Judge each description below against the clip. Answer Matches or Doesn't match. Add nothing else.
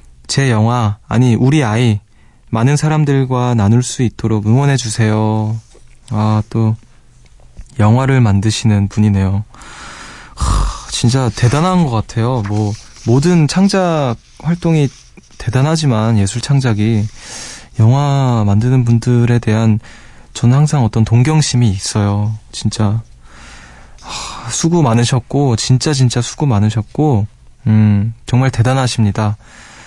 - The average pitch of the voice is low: Matches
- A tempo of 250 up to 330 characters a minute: Doesn't match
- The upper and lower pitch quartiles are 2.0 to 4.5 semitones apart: Matches